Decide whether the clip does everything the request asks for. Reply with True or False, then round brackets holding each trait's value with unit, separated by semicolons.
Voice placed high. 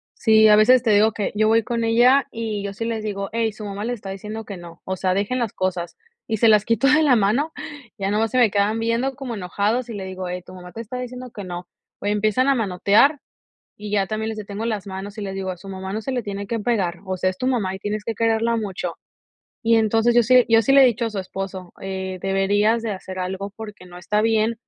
True (215 Hz)